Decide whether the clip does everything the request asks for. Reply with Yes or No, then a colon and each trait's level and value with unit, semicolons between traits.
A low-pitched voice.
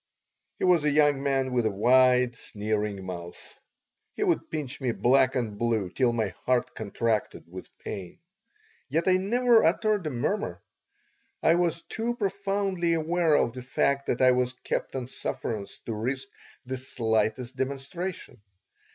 Yes: low, 130 Hz